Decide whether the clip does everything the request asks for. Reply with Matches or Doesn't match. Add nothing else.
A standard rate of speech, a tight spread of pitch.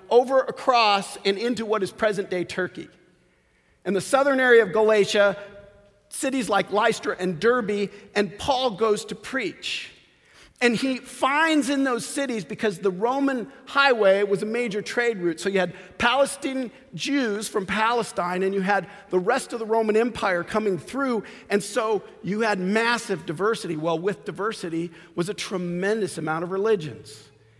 Doesn't match